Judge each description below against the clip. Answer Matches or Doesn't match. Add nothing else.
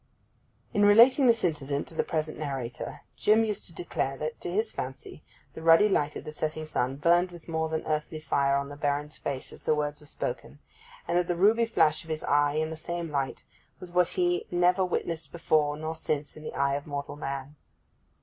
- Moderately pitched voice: Matches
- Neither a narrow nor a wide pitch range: Matches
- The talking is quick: Matches